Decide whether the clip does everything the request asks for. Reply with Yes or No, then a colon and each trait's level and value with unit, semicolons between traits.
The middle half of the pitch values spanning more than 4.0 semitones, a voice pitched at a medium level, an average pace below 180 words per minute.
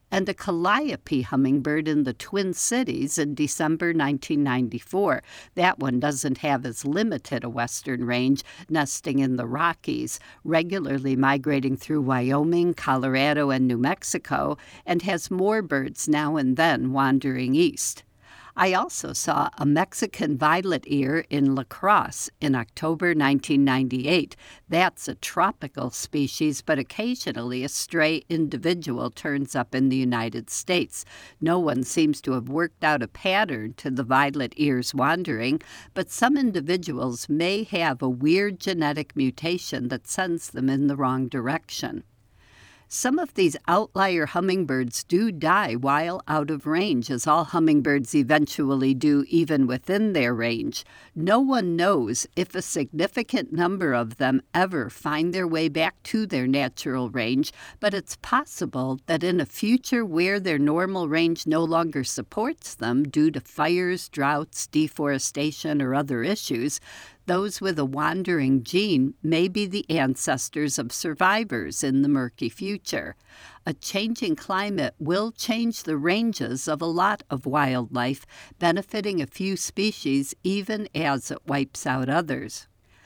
Yes: average, 5.2 semitones; medium, 150 Hz; average, 145 wpm